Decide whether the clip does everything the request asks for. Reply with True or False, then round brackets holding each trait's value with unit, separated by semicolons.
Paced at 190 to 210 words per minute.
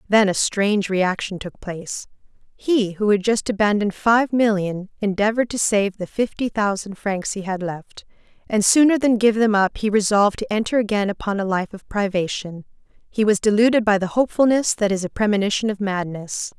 False (180 wpm)